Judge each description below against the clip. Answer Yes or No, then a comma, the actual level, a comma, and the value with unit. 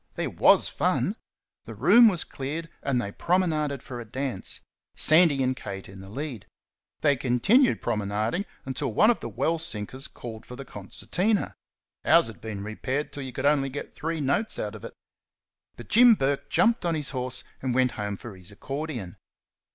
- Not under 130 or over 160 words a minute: No, average, 180 wpm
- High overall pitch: No, low, 135 Hz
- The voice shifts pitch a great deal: Yes, wide, 6.4 semitones